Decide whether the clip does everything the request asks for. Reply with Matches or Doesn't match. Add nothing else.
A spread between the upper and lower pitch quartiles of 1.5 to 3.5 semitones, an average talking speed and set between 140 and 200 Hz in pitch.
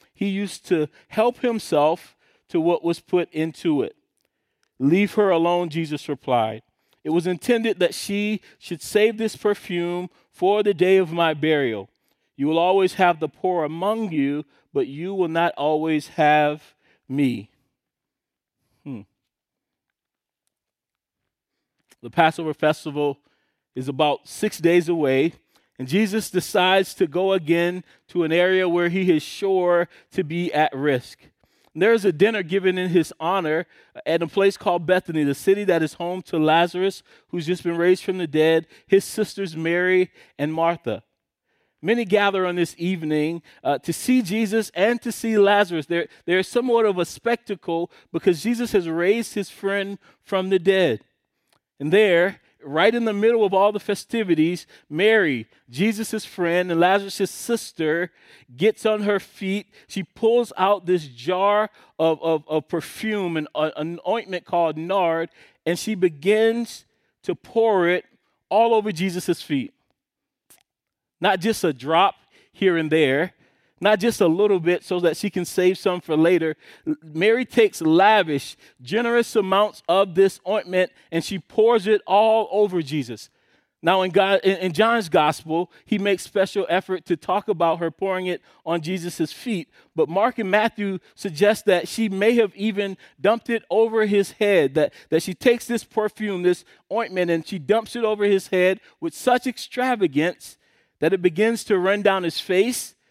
Doesn't match